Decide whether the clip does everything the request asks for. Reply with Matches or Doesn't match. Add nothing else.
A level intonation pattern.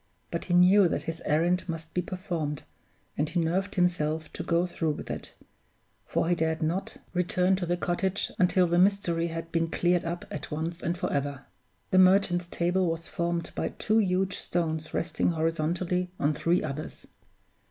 Matches